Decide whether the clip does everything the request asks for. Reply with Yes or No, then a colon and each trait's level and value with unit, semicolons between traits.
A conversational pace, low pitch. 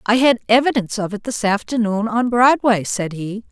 No: average, 190 wpm; high, 220 Hz